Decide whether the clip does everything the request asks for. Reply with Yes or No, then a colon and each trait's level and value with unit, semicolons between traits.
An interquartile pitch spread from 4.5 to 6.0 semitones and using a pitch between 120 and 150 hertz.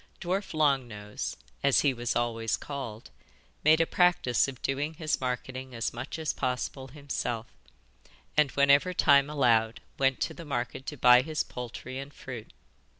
No: average, 3.3 semitones; low, 135 Hz